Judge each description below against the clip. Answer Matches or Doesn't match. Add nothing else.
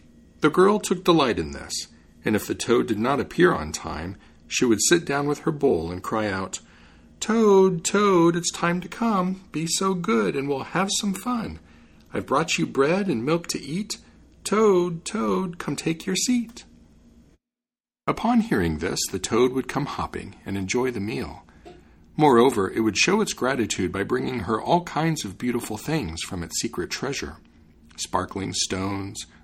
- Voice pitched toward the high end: Doesn't match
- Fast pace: Doesn't match